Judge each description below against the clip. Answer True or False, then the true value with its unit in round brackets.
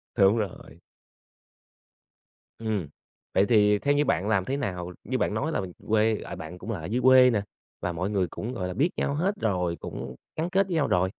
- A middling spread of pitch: False (6.0 semitones)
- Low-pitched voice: True (105 Hz)